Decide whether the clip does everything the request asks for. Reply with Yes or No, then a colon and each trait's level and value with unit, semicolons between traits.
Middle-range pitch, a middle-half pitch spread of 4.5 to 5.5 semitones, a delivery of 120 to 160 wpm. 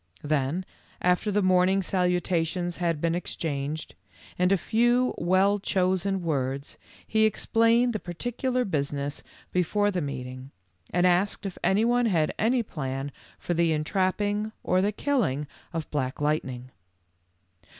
Yes: medium, 180 Hz; average, 5.2 semitones; slow, 135 wpm